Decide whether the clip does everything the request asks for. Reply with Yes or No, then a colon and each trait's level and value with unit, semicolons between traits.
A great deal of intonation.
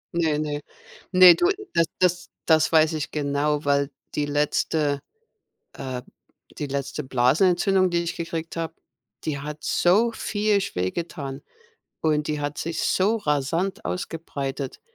No: average, 3.4 semitones